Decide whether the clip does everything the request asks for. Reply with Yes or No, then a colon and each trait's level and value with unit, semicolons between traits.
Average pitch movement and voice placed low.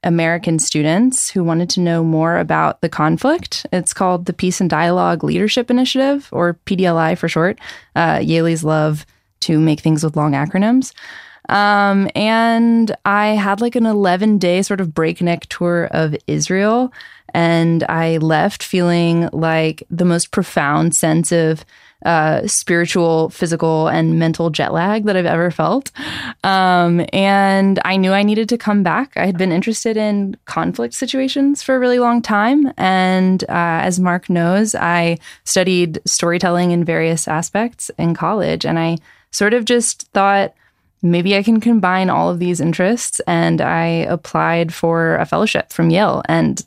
No: average, 3.8 semitones; medium, 180 Hz